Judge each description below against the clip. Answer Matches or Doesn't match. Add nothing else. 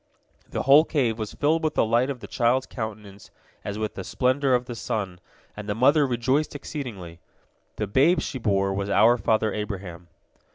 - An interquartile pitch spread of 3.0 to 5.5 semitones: Matches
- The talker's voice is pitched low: Matches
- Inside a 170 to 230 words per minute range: Matches